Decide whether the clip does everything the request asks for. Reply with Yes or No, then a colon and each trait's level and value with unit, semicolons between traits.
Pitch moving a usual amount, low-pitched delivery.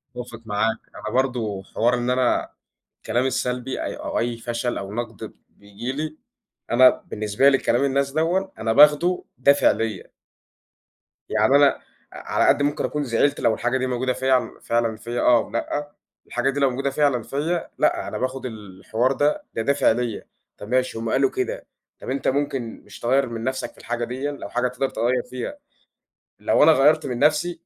Yes: average, 3.2 semitones; low, 125 Hz